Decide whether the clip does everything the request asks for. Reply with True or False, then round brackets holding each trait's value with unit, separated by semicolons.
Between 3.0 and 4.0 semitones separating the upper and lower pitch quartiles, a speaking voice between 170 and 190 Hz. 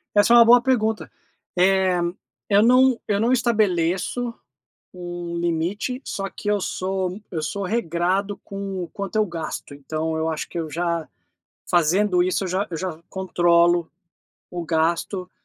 True (3.3 semitones; 185 Hz)